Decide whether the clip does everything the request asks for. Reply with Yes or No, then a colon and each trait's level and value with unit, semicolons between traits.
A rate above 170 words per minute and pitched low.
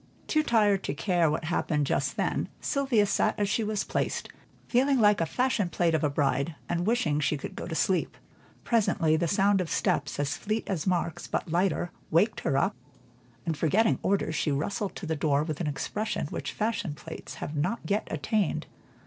No: average, 190 wpm; medium, 175 Hz